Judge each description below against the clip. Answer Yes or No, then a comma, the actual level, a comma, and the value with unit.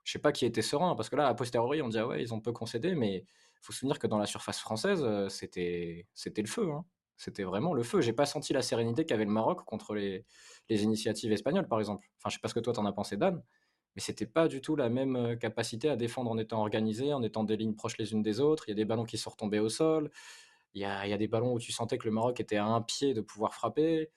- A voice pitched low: Yes, low, 110 Hz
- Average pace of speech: No, fast, 295 wpm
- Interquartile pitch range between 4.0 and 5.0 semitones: No, average, 3.4 semitones